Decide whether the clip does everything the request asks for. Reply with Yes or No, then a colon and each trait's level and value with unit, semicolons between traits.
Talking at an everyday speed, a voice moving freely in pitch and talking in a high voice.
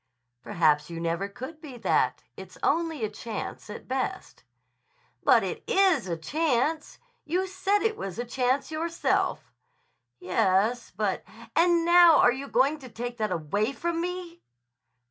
Yes: average, 145 wpm; wide, 8.9 semitones; very high, 255 Hz